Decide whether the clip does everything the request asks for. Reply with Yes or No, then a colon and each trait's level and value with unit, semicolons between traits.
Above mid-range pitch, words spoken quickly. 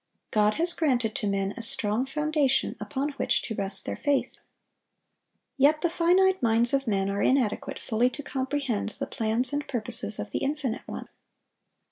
No: very high, 255 Hz; average, 165 wpm